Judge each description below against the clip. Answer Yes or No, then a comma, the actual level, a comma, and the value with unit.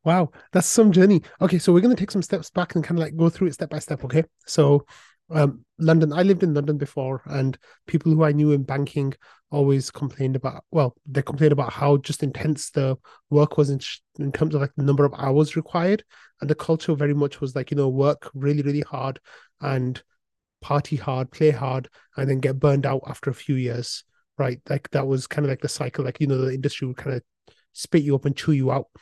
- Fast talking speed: Yes, fast, 235 wpm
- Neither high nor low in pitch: Yes, medium, 145 Hz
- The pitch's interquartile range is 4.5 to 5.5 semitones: No, narrow, 2.4 semitones